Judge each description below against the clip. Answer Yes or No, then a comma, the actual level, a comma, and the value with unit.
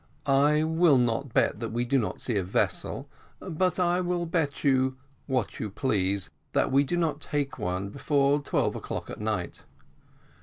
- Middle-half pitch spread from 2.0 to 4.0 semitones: No, wide, 5.5 semitones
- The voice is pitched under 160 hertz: Yes, low, 135 Hz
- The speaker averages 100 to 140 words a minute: No, average, 165 wpm